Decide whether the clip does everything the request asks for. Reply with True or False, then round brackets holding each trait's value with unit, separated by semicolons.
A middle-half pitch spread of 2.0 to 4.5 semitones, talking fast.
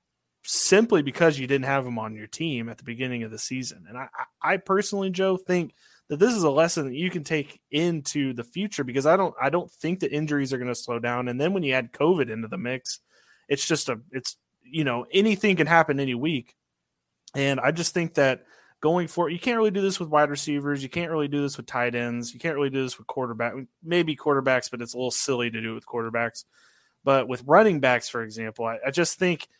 False (5.2 semitones; 240 wpm)